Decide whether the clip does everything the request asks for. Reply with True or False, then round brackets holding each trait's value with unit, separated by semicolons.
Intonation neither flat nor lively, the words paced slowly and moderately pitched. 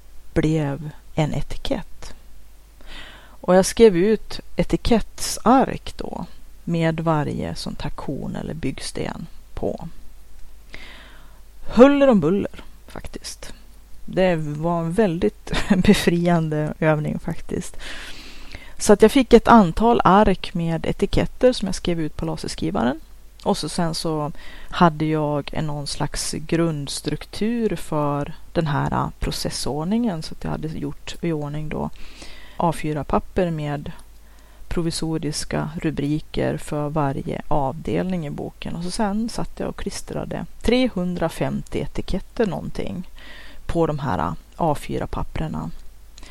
True (4.6 semitones; 110 wpm; 165 Hz)